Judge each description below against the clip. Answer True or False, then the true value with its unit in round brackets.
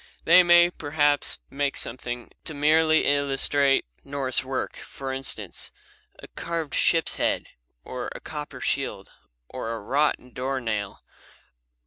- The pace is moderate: False (125 wpm)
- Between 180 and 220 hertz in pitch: False (140 Hz)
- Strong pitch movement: False (3.2 semitones)